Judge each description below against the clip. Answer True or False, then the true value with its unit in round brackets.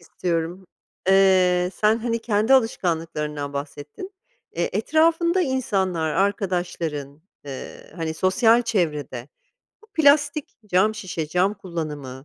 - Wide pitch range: True (6.0 semitones)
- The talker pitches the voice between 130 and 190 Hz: True (185 Hz)